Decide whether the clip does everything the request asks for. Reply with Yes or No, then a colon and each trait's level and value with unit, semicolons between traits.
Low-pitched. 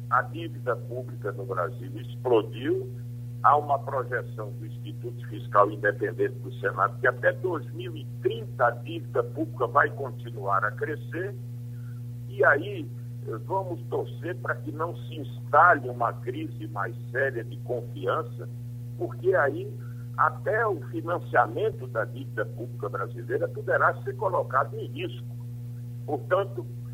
Yes: low, 120 Hz